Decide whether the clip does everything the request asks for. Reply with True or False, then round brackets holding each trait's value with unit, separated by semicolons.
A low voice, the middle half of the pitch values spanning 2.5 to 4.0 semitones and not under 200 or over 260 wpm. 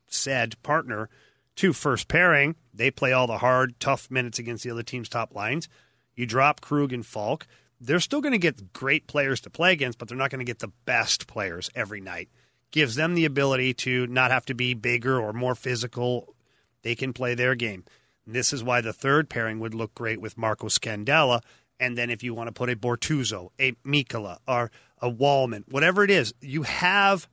True (125 Hz; 3.1 semitones; 205 wpm)